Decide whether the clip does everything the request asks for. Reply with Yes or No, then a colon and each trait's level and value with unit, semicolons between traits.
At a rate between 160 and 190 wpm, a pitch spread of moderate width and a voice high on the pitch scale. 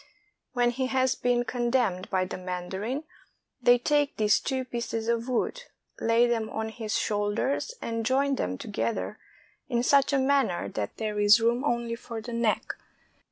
Yes: average, 165 wpm; average, 3.2 semitones; high, 235 Hz